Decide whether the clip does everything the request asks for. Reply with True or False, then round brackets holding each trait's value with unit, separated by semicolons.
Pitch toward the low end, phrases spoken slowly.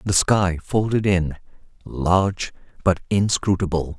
True (90 Hz; 105 wpm)